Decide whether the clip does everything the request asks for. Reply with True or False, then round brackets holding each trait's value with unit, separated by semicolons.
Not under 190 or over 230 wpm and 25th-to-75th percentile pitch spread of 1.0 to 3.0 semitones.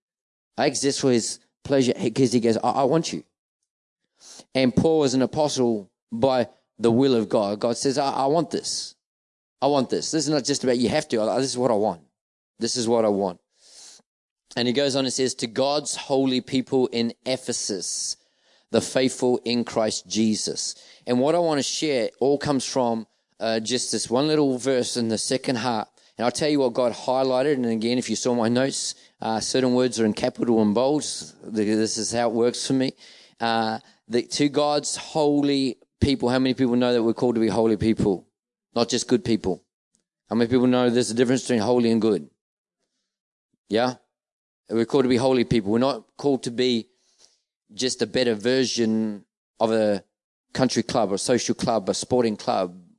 True (195 wpm; 2.6 semitones)